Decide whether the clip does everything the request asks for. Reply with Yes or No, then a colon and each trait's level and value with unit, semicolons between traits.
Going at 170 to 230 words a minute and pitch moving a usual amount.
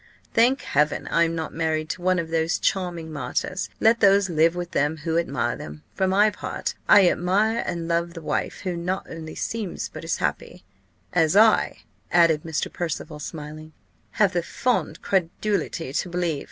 Yes: average, 175 wpm; average, 3.0 semitones